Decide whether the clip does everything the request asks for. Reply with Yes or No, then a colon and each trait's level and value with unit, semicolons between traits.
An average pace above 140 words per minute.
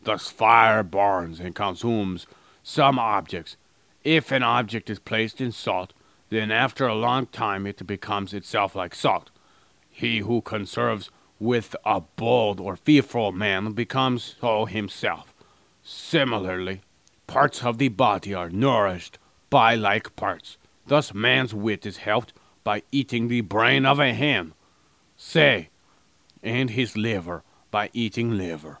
No: slow, 135 wpm